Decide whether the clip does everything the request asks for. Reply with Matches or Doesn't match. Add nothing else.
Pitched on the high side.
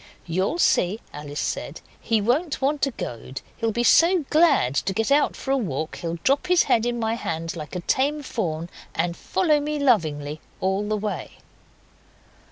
Matches